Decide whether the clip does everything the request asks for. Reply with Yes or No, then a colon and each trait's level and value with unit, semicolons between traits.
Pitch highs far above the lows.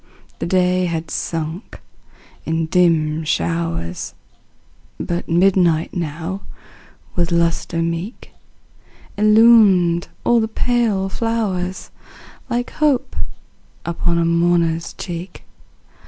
No: average, 3.0 semitones